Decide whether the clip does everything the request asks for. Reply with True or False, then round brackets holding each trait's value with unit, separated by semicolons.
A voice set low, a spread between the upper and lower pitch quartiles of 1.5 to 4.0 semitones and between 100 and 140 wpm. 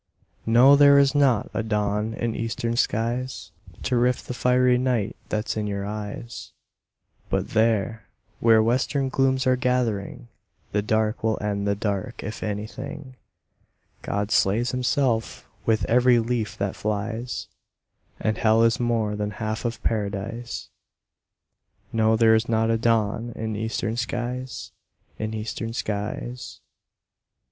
True (115 Hz; 2.5 semitones; 135 wpm)